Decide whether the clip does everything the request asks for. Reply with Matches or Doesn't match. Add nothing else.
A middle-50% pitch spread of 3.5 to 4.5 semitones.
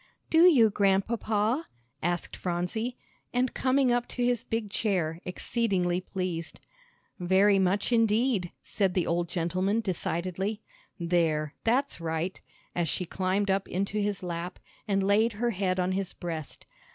Matches